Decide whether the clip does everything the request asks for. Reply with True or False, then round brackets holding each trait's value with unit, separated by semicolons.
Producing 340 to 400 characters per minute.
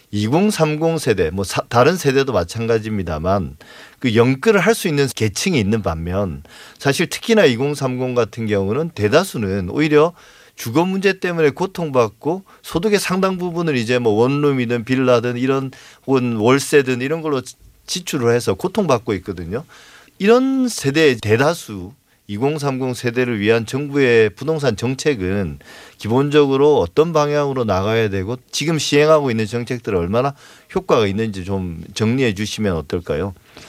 False (300 characters per minute)